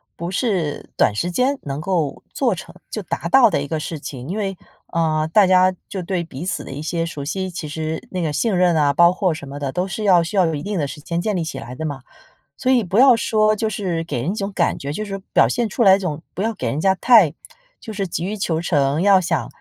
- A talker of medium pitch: Yes, medium, 175 Hz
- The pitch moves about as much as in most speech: Yes, average, 4.2 semitones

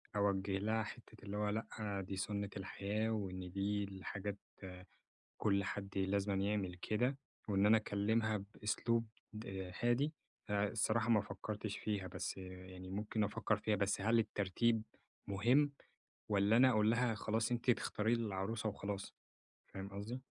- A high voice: No, low, 105 Hz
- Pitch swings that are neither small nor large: No, narrow, 2.2 semitones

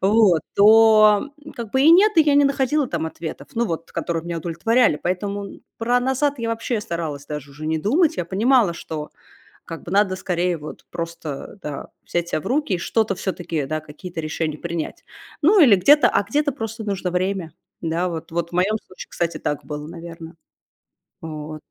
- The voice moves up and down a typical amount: No, wide, 5.7 semitones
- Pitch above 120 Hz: Yes, medium, 185 Hz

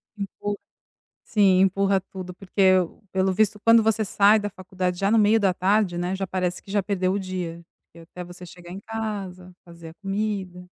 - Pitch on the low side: No, high, 190 Hz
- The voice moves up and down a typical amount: No, narrow, 2.3 semitones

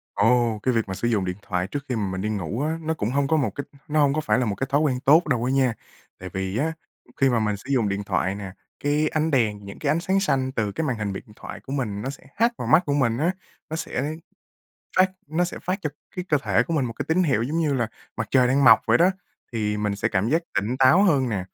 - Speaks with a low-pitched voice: Yes, low, 130 Hz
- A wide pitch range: Yes, wide, 6.2 semitones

